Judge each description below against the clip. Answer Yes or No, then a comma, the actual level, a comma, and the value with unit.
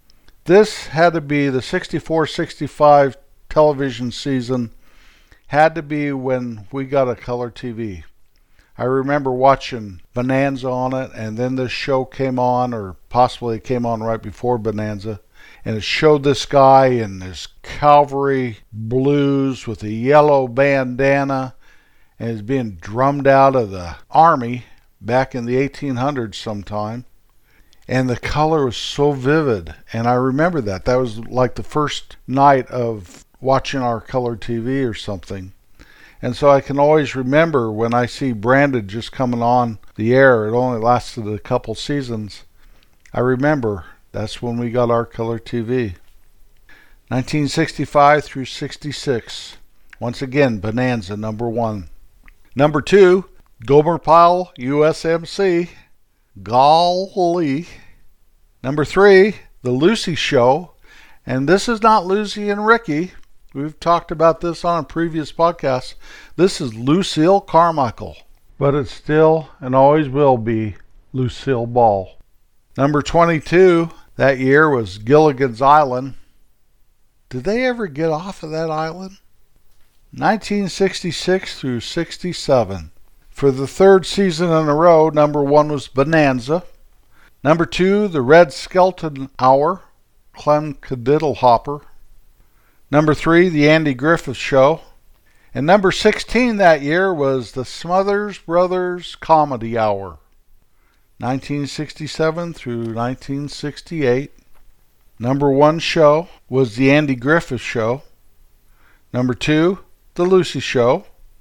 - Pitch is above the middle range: No, low, 135 Hz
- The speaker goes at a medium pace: No, slow, 125 wpm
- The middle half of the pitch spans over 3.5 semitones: Yes, average, 4.7 semitones